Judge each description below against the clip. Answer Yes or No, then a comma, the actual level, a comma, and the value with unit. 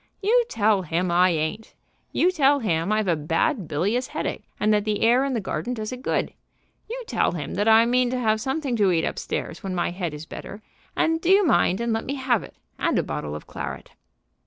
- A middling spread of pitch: No, wide, 6.2 semitones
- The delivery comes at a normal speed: No, fast, 230 wpm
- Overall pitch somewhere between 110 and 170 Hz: No, high, 215 Hz